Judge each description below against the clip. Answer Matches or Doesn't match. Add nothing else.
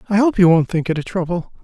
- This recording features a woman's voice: Doesn't match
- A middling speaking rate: Doesn't match